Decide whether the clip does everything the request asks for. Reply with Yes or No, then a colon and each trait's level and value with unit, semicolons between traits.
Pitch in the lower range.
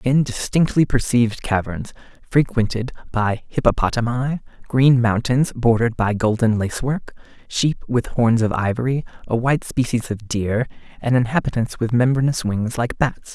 Yes: low, 120 Hz